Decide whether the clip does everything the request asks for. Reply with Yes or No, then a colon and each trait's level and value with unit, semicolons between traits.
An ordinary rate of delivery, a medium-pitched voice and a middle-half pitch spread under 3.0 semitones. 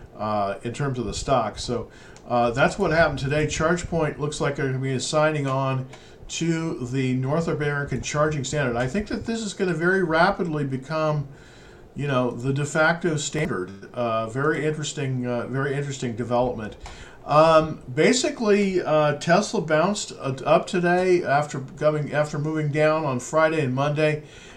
No: average, 160 wpm; medium, 150 Hz; average, 3.3 semitones